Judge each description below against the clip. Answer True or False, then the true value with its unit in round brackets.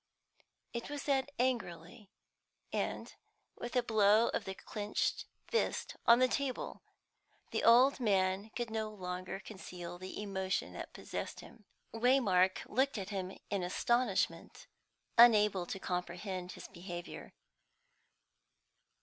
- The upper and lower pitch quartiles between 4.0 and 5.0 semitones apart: True (4.3 semitones)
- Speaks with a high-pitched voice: True (205 Hz)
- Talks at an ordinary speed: False (120 wpm)